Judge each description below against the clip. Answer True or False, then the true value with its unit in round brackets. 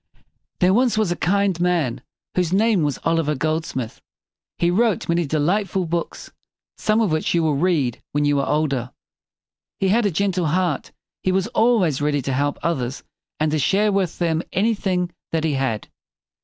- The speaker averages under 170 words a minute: False (185 wpm)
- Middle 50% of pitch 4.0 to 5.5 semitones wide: True (4.5 semitones)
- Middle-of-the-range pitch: True (170 Hz)